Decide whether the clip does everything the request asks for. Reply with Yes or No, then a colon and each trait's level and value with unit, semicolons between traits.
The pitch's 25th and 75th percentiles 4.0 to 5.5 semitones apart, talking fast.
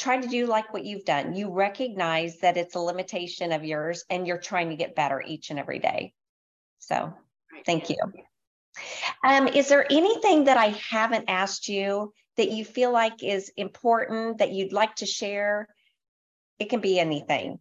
No: average, 4.4 semitones; average, 175 wpm